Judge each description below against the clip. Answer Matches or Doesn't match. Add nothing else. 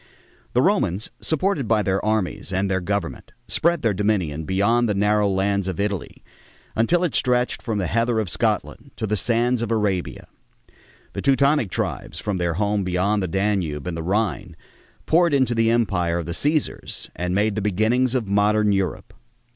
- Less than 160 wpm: Doesn't match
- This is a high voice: Doesn't match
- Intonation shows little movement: Doesn't match